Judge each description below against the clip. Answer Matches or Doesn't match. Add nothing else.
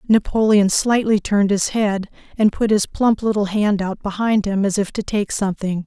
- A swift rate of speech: Doesn't match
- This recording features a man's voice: Doesn't match